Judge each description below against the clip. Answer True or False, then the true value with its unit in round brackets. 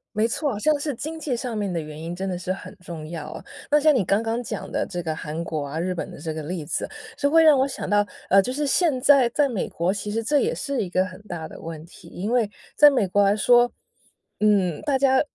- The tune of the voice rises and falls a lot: True (7.1 semitones)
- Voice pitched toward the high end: True (205 Hz)